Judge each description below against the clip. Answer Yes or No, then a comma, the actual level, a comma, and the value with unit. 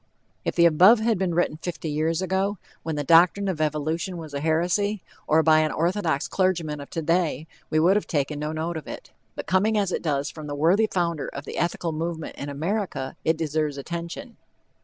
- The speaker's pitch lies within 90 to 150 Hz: No, medium, 165 Hz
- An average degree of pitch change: Yes, average, 3.2 semitones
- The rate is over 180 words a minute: Yes, average, 200 wpm